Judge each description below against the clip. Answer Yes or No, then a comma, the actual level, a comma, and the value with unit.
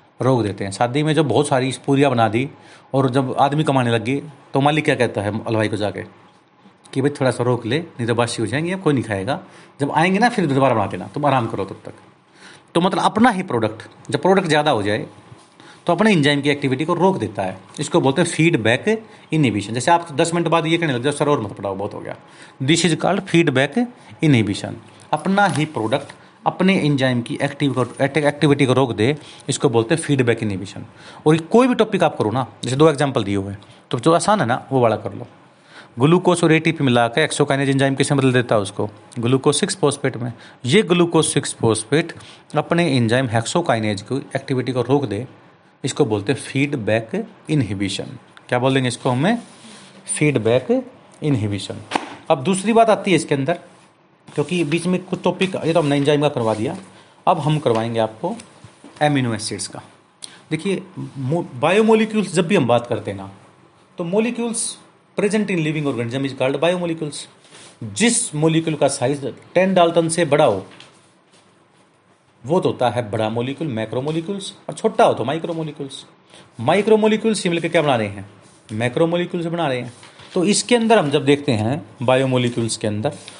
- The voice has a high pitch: No, medium, 145 Hz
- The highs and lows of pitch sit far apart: Yes, wide, 5.8 semitones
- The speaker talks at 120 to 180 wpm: No, fast, 190 wpm